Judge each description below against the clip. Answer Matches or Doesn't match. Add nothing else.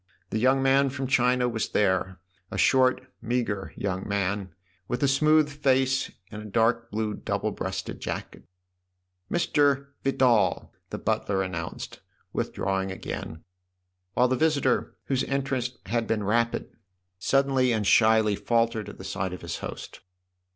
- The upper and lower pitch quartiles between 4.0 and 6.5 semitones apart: Matches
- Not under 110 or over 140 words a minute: Doesn't match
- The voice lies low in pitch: Matches